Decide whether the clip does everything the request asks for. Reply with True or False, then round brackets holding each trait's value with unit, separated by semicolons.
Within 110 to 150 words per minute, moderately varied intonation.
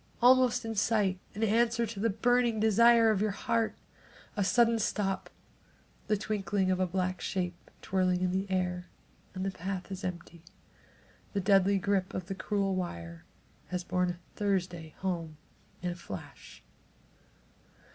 True (145 wpm; 3.0 semitones)